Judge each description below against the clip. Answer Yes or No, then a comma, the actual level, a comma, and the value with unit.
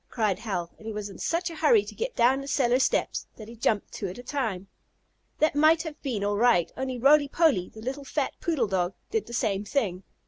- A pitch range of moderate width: No, wide, 6.0 semitones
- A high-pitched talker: Yes, high, 240 Hz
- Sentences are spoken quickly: Yes, fast, 235 wpm